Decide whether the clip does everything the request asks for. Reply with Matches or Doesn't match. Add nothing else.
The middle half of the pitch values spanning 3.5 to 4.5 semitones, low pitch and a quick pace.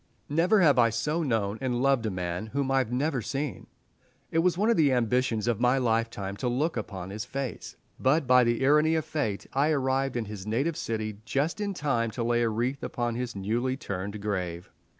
Matches